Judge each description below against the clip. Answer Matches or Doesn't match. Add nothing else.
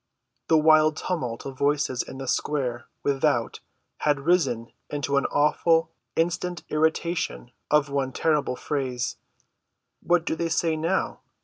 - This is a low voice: Doesn't match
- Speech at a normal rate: Doesn't match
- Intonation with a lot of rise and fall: Doesn't match